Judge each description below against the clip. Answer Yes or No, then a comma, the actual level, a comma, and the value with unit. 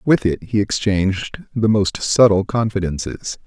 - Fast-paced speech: No, average, 140 wpm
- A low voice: Yes, low, 105 Hz